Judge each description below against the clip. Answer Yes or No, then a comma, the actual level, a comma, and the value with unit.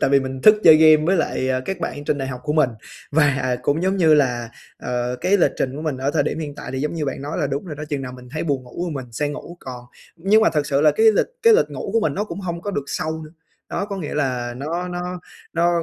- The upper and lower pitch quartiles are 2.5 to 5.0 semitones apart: Yes, average, 4.3 semitones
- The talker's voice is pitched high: No, medium, 150 Hz